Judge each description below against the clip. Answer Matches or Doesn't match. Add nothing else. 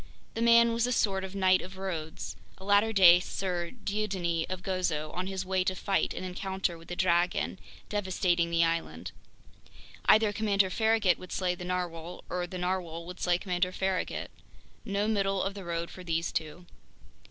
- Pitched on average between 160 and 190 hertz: Matches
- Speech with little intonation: Matches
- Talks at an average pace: Matches